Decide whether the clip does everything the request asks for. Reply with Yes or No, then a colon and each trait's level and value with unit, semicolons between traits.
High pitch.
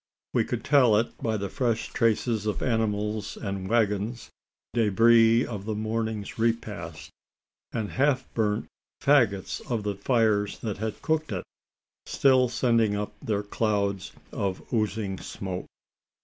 No: low, 110 Hz